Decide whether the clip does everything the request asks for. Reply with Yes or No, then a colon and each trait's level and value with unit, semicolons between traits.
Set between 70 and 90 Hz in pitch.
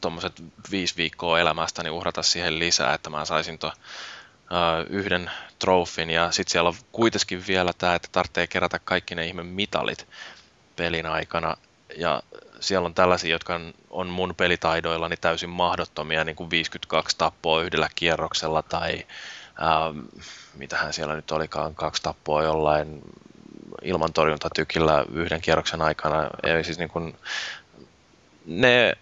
Yes: very low, 85 Hz